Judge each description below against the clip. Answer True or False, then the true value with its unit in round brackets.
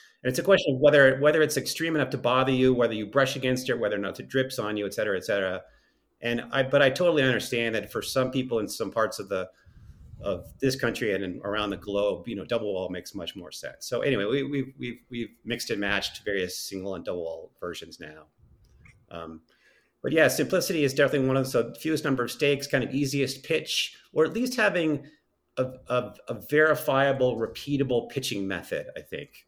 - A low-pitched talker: True (130 Hz)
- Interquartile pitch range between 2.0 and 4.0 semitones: True (3.3 semitones)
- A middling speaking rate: False (220 wpm)